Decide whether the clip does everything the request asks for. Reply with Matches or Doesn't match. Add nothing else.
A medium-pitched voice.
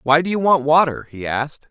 Matches